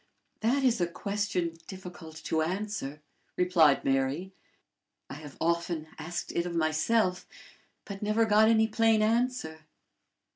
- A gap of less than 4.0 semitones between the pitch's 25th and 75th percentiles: No, average, 5.2 semitones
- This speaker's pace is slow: Yes, slow, 125 wpm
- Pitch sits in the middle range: Yes, medium, 180 Hz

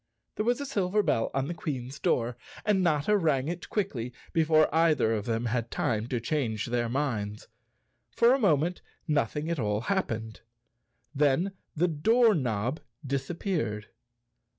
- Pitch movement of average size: No, wide, 7.0 semitones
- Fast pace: No, average, 150 wpm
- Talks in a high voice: No, medium, 145 Hz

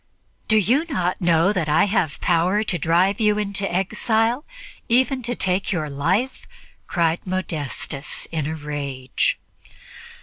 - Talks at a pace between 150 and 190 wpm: No, slow, 135 wpm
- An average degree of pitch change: Yes, average, 5.0 semitones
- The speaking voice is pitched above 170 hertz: Yes, medium, 185 Hz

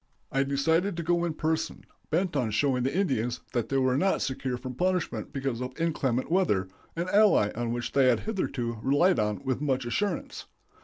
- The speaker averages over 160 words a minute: Yes, average, 185 wpm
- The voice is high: No, low, 135 Hz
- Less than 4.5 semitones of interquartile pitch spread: No, wide, 5.4 semitones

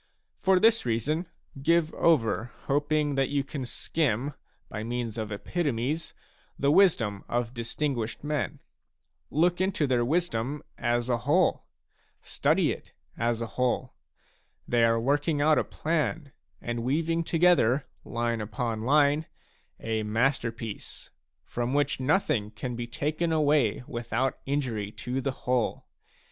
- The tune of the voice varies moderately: Yes, average, 4.5 semitones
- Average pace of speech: No, slow, 130 wpm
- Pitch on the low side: Yes, low, 130 Hz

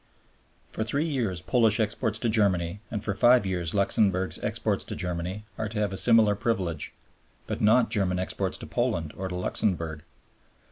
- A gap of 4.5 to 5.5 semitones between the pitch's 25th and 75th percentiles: No, average, 3.4 semitones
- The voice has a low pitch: Yes, low, 100 Hz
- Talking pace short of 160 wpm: No, average, 170 wpm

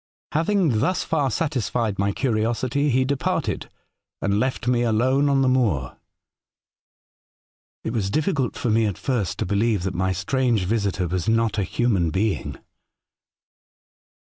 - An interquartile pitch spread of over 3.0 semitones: Yes, average, 4.7 semitones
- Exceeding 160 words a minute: No, average, 150 wpm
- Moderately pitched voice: No, low, 115 Hz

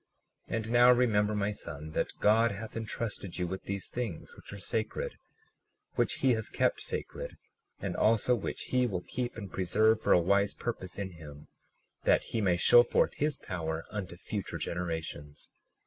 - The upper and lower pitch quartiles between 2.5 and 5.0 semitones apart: Yes, average, 4.2 semitones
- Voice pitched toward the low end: Yes, low, 100 Hz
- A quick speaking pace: No, average, 175 wpm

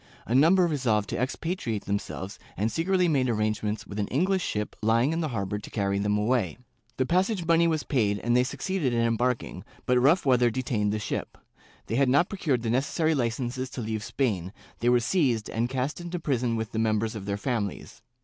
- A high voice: No, low, 120 Hz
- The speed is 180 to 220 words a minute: Yes, fast, 205 wpm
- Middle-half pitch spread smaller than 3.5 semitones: No, average, 5.1 semitones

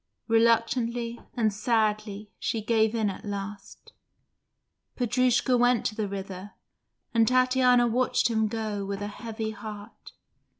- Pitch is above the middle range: Yes, high, 220 Hz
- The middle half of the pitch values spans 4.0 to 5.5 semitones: No, narrow, 2.4 semitones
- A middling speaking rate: No, slow, 125 wpm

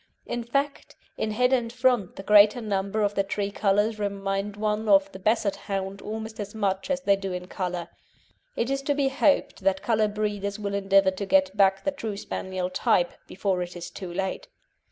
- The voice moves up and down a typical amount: No, narrow, 2.2 semitones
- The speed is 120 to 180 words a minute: No, average, 195 wpm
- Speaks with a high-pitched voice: Yes, high, 200 Hz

